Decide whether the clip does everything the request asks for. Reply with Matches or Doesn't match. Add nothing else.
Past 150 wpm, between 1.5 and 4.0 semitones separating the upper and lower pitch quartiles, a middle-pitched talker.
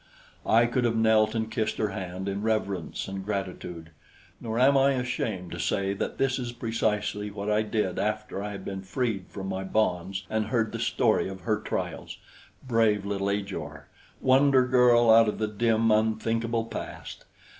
Doesn't match